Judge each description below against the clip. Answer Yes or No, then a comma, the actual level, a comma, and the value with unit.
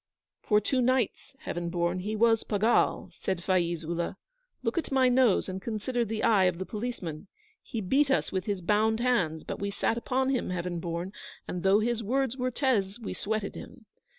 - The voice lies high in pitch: Yes, high, 210 Hz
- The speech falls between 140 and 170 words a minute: No, average, 190 wpm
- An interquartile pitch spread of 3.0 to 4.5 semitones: No, average, 4.9 semitones